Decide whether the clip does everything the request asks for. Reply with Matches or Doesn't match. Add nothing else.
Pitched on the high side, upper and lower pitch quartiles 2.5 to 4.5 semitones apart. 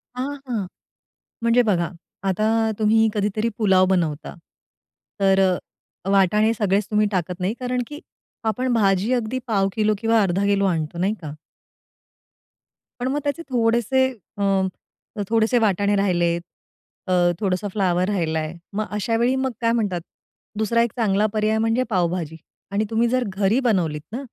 Matches